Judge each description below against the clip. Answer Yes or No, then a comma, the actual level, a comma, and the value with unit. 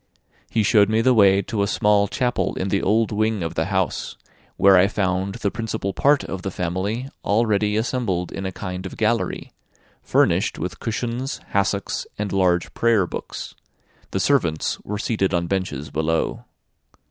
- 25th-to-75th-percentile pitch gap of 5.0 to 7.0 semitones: No, average, 3.1 semitones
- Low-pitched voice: Yes, low, 100 Hz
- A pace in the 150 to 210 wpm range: Yes, average, 165 wpm